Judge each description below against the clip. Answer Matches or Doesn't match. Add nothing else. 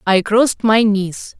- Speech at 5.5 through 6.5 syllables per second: Doesn't match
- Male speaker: Doesn't match